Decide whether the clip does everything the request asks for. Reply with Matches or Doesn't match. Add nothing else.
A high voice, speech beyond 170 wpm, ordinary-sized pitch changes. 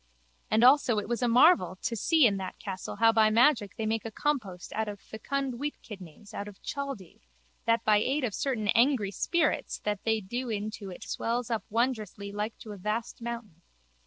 Matches